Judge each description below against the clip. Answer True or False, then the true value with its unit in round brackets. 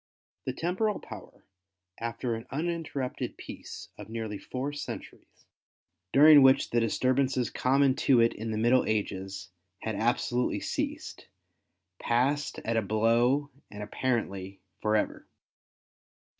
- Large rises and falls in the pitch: False (3.7 semitones)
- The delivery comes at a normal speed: False (120 wpm)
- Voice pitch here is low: True (120 Hz)